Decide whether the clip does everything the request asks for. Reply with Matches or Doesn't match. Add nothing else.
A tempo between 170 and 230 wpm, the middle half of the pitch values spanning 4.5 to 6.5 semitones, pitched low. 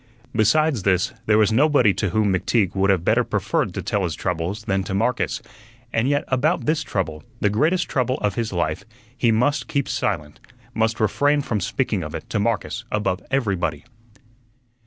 Matches